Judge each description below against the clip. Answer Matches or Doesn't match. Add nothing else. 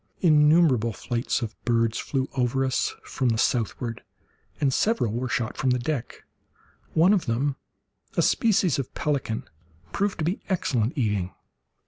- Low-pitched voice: Matches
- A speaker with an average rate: Matches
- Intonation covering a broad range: Doesn't match